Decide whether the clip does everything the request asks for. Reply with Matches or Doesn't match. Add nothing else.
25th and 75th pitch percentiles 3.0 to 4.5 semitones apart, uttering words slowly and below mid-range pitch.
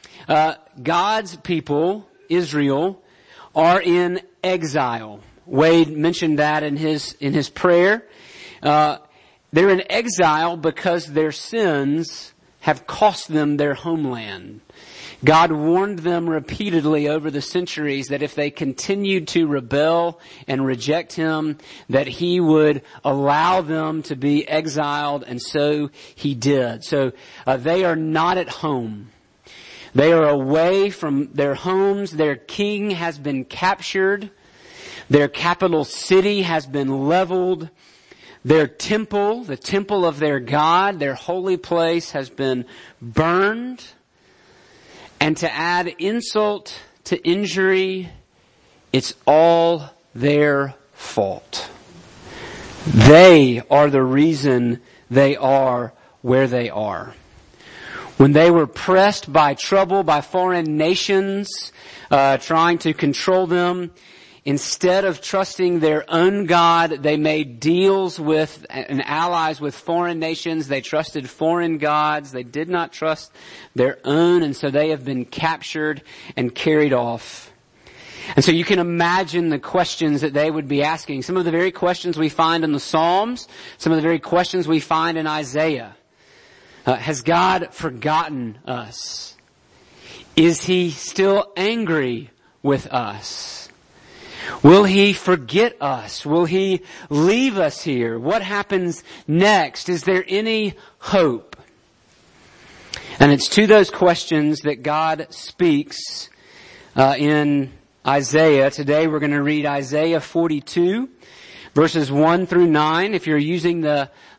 Doesn't match